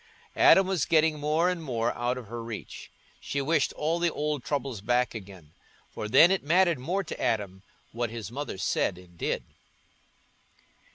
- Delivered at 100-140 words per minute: No, average, 170 wpm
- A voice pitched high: No, low, 130 Hz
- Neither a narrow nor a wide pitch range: No, wide, 6.0 semitones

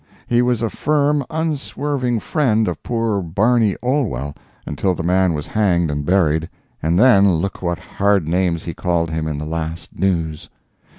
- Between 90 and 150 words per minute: No, average, 165 wpm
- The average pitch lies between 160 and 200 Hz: No, very low, 95 Hz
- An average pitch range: No, wide, 6.5 semitones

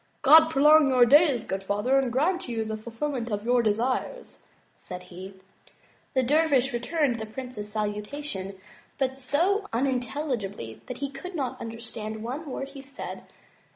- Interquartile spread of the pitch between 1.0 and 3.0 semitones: No, average, 4.4 semitones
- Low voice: No, very high, 255 Hz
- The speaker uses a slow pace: No, average, 155 wpm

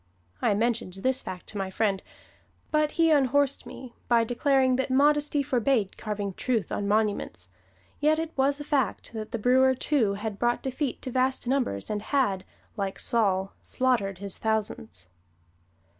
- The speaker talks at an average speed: Yes, average, 160 wpm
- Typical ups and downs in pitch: Yes, average, 4.8 semitones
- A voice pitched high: Yes, high, 240 Hz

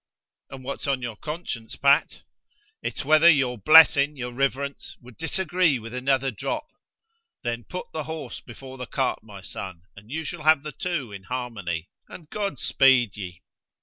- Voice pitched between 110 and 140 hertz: Yes, low, 135 Hz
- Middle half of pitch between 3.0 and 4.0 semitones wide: No, average, 4.6 semitones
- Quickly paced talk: No, average, 165 wpm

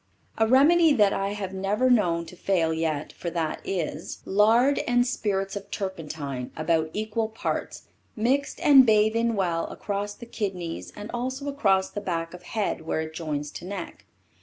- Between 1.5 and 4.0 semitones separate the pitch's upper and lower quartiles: No, average, 5.3 semitones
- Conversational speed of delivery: Yes, average, 170 wpm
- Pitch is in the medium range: No, high, 195 Hz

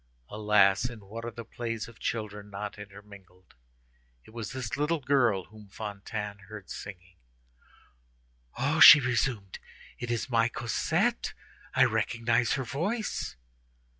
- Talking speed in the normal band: No, slow, 130 wpm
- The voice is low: Yes, low, 110 Hz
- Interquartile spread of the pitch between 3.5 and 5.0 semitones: No, average, 3.0 semitones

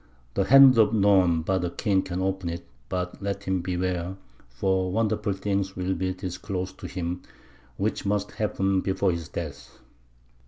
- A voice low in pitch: Yes, very low, 95 Hz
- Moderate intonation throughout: No, narrow, 1.7 semitones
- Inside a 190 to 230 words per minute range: No, average, 160 wpm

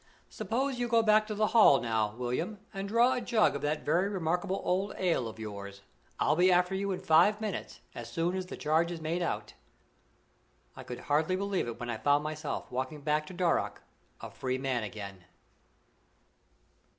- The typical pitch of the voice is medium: Yes, medium, 165 Hz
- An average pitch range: No, wide, 7.3 semitones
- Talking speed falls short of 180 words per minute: No, average, 185 wpm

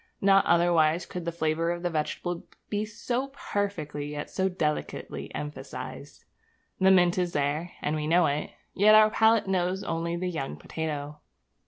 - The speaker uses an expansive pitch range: No, average, 3.7 semitones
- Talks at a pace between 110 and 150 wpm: No, average, 160 wpm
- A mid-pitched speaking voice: Yes, medium, 170 Hz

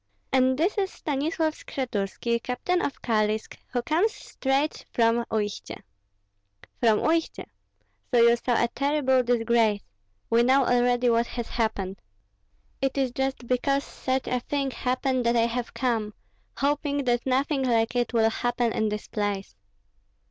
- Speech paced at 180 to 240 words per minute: No, average, 145 wpm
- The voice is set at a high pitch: Yes, high, 245 Hz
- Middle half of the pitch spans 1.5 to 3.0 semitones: Yes, average, 2.7 semitones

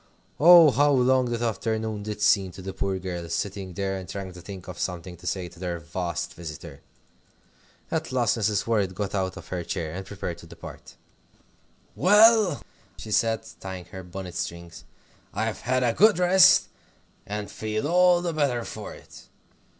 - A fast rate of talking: No, average, 175 wpm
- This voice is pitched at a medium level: No, low, 100 Hz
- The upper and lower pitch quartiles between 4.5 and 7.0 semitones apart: Yes, average, 5.2 semitones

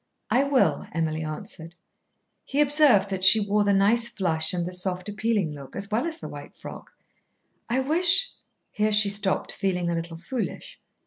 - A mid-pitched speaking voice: No, high, 200 Hz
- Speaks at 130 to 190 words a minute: Yes, average, 180 wpm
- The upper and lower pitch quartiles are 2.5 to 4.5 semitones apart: No, average, 5.1 semitones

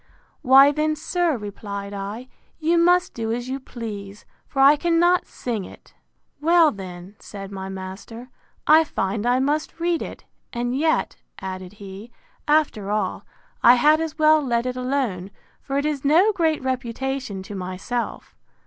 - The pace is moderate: Yes, average, 155 wpm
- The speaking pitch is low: No, very high, 255 Hz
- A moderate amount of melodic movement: No, wide, 7.1 semitones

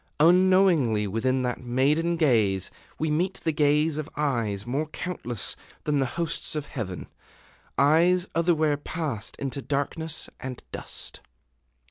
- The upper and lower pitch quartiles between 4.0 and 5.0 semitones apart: Yes, average, 4.7 semitones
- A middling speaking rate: No, slow, 125 wpm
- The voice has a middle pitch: Yes, medium, 145 Hz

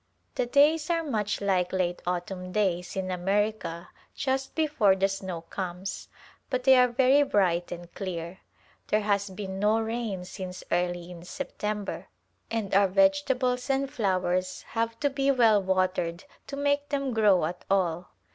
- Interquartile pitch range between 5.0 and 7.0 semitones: Yes, wide, 5.6 semitones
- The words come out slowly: No, average, 155 wpm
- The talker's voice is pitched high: Yes, high, 200 Hz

